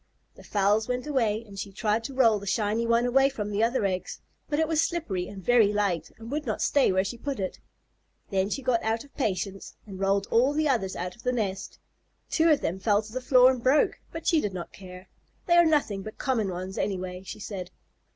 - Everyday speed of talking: No, fast, 230 wpm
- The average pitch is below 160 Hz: No, high, 215 Hz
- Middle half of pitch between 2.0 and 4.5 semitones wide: No, average, 5.0 semitones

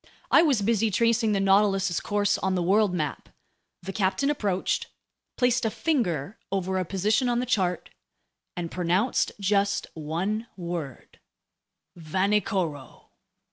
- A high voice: Yes, high, 195 Hz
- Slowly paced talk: Yes, slow, 130 wpm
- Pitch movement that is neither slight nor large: Yes, average, 3.6 semitones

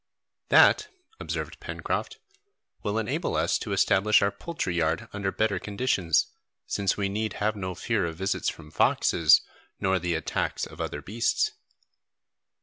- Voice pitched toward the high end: No, low, 100 Hz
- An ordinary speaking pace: Yes, average, 145 wpm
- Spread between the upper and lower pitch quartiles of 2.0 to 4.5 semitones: Yes, average, 3.3 semitones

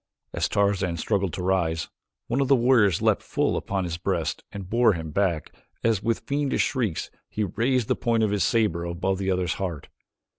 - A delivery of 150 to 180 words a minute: No, average, 190 wpm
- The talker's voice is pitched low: Yes, low, 100 Hz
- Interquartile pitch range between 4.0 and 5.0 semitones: Yes, average, 4.6 semitones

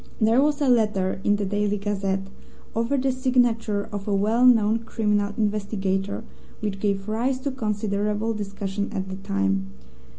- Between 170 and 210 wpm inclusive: No, average, 155 wpm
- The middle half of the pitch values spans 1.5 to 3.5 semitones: Yes, narrow, 2.5 semitones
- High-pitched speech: Yes, high, 210 Hz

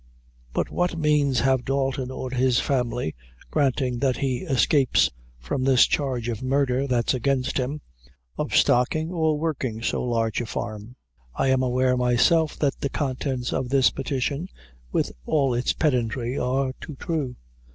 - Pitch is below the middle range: Yes, low, 130 Hz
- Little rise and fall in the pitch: Yes, narrow, 2.2 semitones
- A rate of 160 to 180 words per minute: No, average, 150 wpm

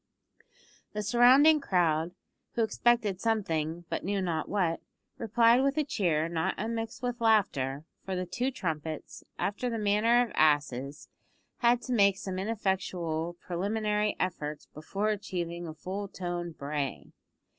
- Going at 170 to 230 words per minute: No, slow, 135 wpm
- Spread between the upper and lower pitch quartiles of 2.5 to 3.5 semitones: No, wide, 5.4 semitones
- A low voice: No, high, 190 Hz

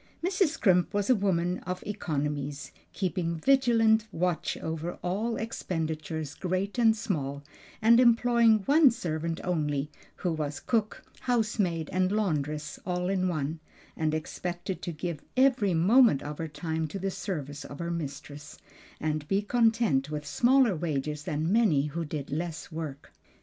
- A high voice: No, medium, 175 Hz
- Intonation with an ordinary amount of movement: No, wide, 5.8 semitones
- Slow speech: No, average, 145 wpm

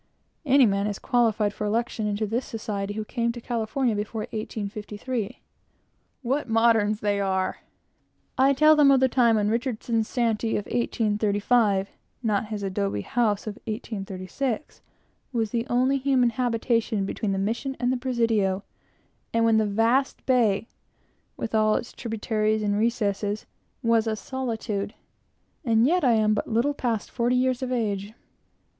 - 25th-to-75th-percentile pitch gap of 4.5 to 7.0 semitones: No, average, 2.8 semitones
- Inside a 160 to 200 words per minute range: No, average, 150 wpm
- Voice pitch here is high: Yes, high, 225 Hz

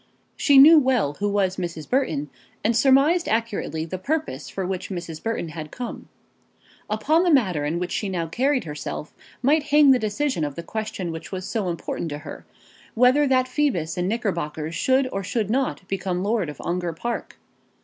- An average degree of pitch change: No, wide, 7.4 semitones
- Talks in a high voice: Yes, high, 200 Hz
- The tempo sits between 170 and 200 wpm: Yes, average, 180 wpm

